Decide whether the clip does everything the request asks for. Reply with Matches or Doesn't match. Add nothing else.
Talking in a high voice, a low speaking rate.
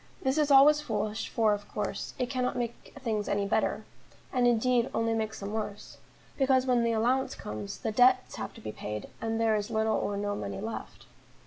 Doesn't match